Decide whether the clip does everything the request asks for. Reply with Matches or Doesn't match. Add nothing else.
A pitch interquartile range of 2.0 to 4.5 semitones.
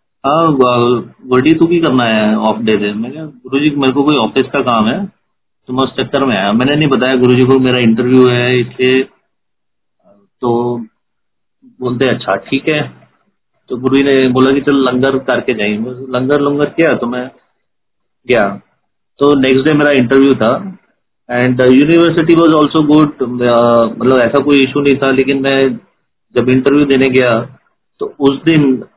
Matches